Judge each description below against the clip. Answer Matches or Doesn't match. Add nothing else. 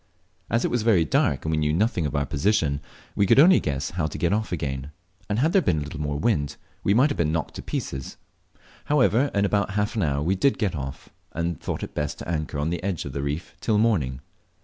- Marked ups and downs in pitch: Matches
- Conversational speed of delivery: Doesn't match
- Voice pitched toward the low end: Matches